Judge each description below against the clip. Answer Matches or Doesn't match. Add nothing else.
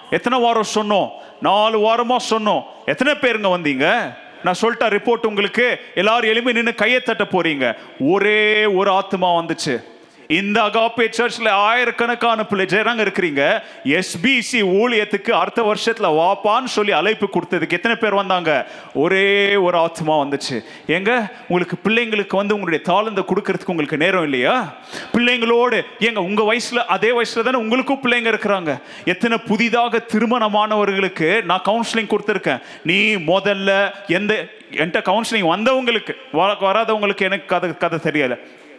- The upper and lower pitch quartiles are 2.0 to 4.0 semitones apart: Matches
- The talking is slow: Doesn't match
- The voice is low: Doesn't match